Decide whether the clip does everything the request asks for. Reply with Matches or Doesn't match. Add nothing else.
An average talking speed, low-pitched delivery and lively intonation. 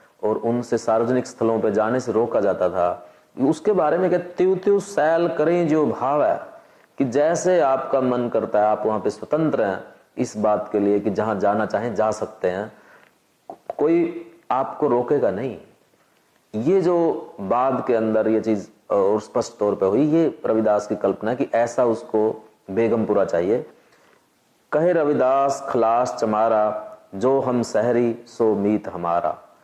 Matches